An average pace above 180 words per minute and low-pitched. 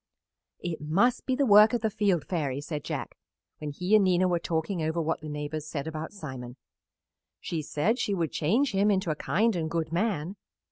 No: average, 200 wpm; medium, 170 Hz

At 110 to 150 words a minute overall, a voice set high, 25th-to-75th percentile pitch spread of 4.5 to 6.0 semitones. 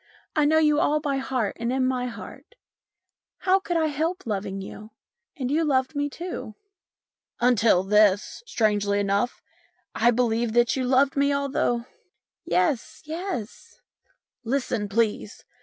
Yes: average, 145 wpm; very high, 250 Hz; average, 5.1 semitones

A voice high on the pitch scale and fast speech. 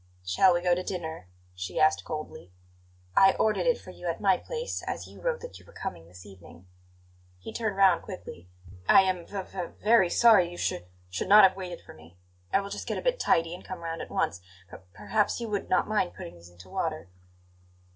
No: medium, 180 Hz; fast, 215 wpm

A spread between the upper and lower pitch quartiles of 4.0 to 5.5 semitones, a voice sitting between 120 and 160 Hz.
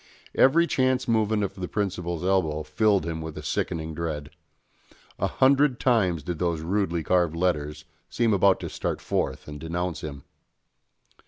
No: average, 4.8 semitones; very low, 90 Hz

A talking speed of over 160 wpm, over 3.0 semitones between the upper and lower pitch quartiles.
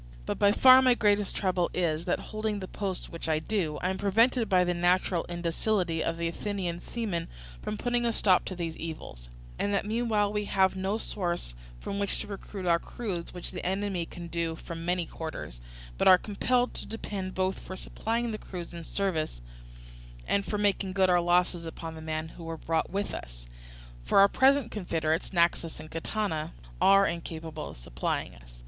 Yes: average, 190 wpm; average, 3.6 semitones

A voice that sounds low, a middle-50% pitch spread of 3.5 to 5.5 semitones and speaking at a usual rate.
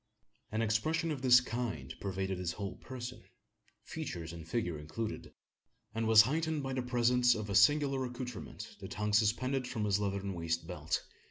Yes: low, 110 Hz; average, 4.7 semitones; average, 165 wpm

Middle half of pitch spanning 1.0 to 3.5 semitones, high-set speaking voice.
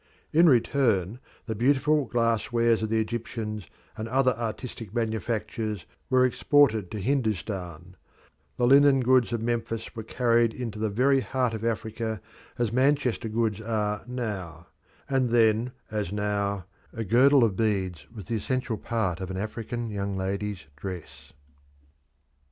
No: average, 2.9 semitones; low, 115 Hz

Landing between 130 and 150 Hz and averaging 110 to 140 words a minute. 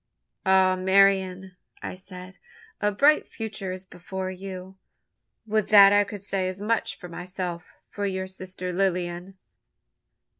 No: high, 190 Hz; slow, 135 wpm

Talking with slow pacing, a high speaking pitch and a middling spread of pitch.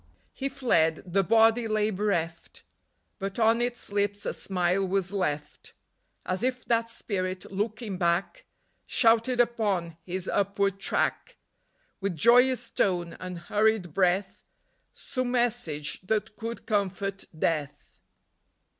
Yes: slow, 120 wpm; high, 200 Hz; average, 4.0 semitones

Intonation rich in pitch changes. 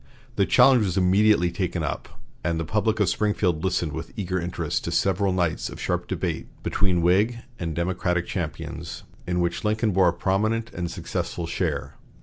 No: average, 3.2 semitones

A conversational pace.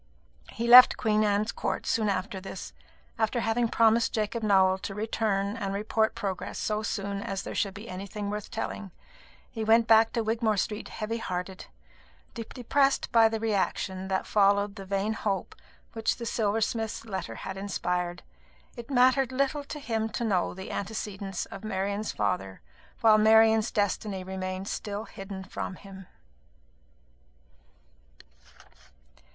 Yes: average, 145 wpm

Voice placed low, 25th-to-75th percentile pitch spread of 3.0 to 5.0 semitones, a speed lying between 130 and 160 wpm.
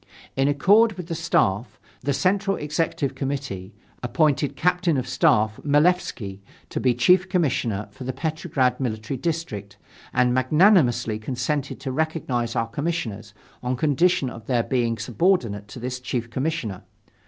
No: low, 130 Hz; wide, 5.5 semitones; average, 140 wpm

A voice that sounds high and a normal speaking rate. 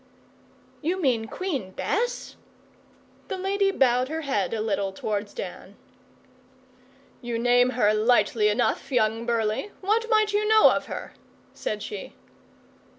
No: high, 245 Hz; slow, 130 wpm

